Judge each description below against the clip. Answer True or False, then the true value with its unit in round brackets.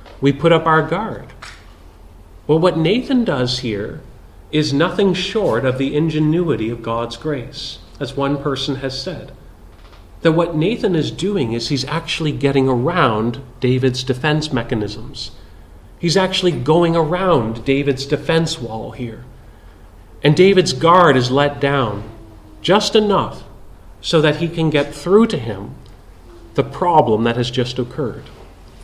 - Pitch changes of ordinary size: False (6.7 semitones)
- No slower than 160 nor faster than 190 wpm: False (140 wpm)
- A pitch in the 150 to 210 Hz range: False (135 Hz)